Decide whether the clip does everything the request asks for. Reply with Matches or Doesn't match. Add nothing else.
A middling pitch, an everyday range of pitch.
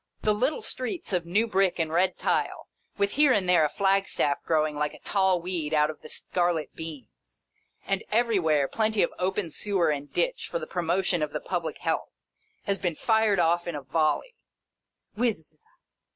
Matches